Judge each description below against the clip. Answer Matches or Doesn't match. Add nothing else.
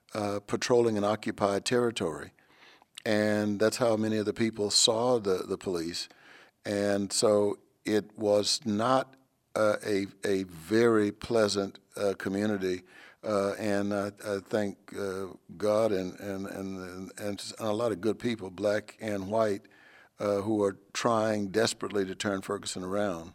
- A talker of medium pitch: Doesn't match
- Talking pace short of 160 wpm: Matches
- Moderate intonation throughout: Doesn't match